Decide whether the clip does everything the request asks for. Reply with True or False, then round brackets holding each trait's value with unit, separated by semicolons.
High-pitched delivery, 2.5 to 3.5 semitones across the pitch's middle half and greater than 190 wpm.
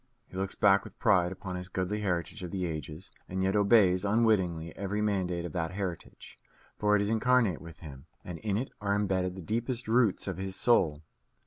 False (95 Hz; 2.8 semitones; 200 wpm)